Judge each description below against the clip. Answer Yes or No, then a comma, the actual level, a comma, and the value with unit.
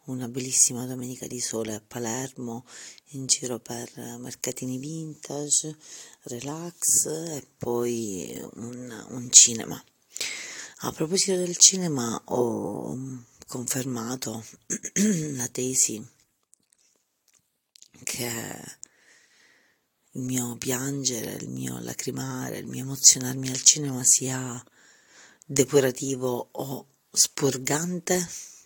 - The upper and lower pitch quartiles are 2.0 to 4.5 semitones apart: Yes, average, 2.9 semitones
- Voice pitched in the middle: No, low, 130 Hz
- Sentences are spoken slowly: Yes, slow, 90 wpm